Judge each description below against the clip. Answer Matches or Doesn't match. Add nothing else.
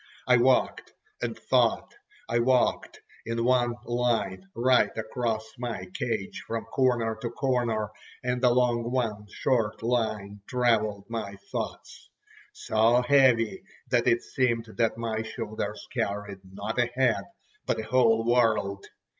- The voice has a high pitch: Doesn't match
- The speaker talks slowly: Matches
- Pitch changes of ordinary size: Doesn't match